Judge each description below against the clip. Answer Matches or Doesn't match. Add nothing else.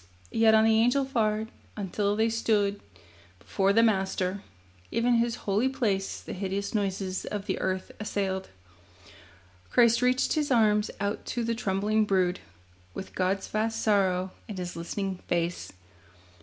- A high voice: Matches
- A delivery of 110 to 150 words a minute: Matches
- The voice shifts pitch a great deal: Doesn't match